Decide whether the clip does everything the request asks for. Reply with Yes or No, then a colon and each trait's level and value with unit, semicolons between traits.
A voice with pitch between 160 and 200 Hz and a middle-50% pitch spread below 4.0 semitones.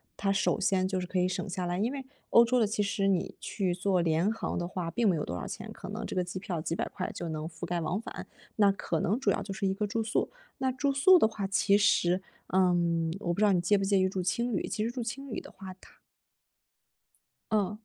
Yes: high, 195 Hz; average, 3.4 semitones